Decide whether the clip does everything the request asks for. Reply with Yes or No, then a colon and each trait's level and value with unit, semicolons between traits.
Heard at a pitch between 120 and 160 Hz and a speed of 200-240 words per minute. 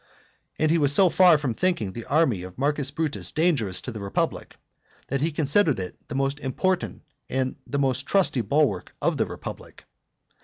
No: medium, 140 Hz; average, 180 wpm